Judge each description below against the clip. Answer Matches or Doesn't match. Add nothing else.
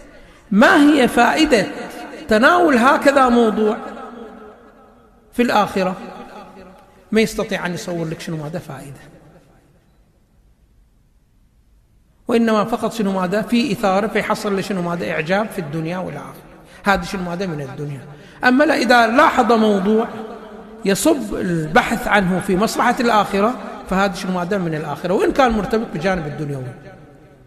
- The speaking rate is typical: Matches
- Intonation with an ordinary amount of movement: Matches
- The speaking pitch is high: Matches